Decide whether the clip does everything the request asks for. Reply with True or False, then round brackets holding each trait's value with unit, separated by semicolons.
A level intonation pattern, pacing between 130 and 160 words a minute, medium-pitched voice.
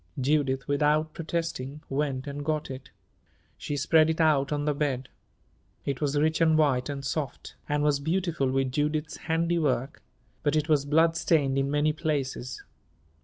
True (2.3 semitones; 155 wpm; 145 Hz)